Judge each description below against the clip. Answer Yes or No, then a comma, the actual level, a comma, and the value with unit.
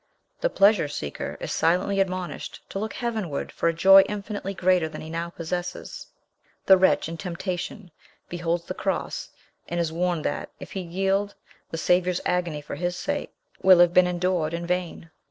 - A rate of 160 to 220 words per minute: Yes, average, 170 wpm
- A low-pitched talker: No, medium, 180 Hz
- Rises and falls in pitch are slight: Yes, narrow, 2.1 semitones